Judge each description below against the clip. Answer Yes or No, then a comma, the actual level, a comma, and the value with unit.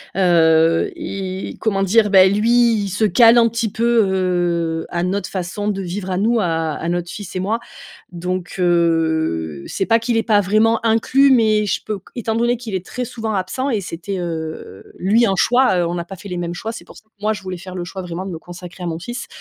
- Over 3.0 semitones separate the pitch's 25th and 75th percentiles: Yes, average, 4.0 semitones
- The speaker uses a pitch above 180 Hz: Yes, high, 190 Hz